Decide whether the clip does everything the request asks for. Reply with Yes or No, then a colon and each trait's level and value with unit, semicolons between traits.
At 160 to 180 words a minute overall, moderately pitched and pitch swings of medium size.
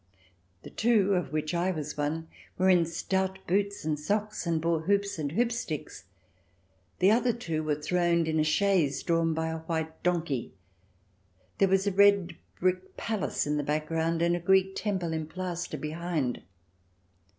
Yes: average, 165 wpm; medium, 170 Hz; average, 3.3 semitones